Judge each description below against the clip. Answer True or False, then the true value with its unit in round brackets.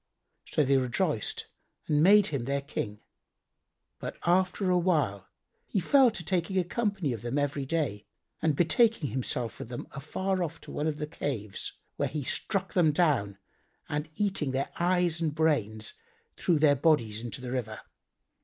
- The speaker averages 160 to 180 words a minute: True (165 wpm)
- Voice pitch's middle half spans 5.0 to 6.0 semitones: True (5.6 semitones)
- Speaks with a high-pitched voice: False (150 Hz)